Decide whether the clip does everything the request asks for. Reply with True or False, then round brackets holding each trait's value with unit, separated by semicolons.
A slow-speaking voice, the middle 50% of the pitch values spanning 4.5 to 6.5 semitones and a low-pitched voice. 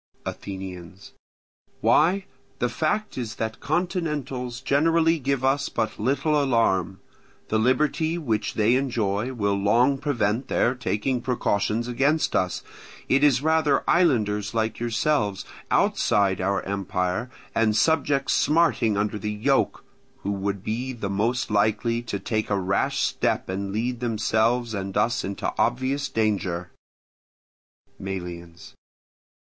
True (125 wpm; 5.2 semitones; 115 Hz)